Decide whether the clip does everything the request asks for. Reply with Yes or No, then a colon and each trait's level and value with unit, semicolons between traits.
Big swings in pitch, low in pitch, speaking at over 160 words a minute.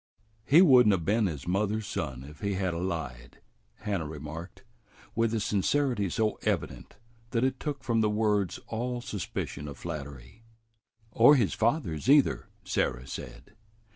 No: wide, 6.5 semitones; low, 100 Hz; average, 155 wpm